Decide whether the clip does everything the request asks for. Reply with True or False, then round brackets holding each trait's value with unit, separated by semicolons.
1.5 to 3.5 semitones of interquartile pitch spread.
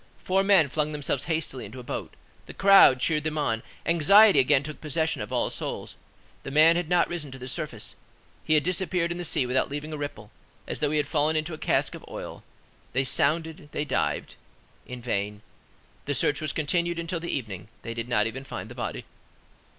False (4.0 semitones)